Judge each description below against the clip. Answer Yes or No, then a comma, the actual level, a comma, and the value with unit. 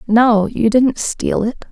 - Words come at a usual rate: Yes, average, 175 wpm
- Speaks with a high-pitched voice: Yes, high, 230 Hz